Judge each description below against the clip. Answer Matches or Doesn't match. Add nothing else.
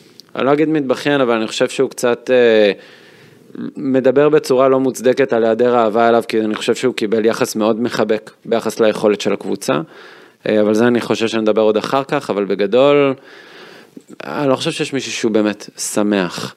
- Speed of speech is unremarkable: Doesn't match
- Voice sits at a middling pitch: Doesn't match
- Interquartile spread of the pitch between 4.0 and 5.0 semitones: Doesn't match